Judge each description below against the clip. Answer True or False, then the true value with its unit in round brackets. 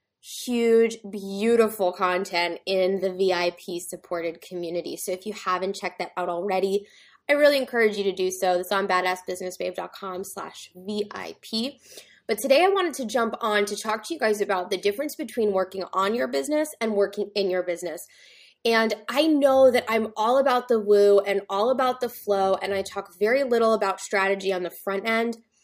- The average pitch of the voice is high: True (200 Hz)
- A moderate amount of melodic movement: True (3.6 semitones)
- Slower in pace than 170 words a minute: False (180 wpm)